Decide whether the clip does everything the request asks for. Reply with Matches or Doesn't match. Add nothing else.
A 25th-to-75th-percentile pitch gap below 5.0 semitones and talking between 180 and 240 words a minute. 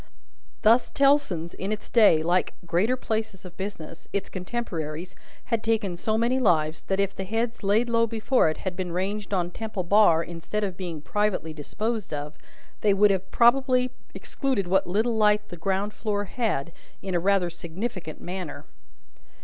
Doesn't match